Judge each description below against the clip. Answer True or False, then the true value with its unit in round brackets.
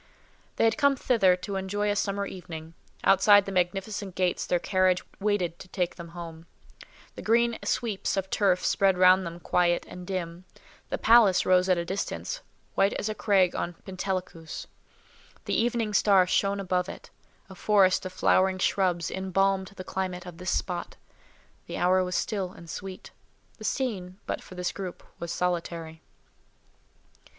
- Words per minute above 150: True (160 wpm)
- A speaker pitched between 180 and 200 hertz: True (185 Hz)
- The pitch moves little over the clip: True (1.9 semitones)